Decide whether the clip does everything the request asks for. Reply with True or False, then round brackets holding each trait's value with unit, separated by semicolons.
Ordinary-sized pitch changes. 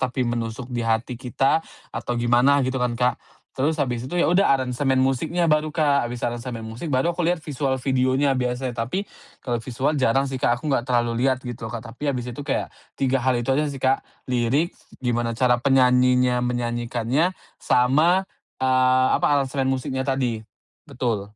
False (2.2 semitones)